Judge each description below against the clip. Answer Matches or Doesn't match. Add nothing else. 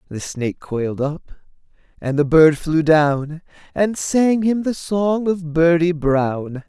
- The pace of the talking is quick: Doesn't match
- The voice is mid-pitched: Matches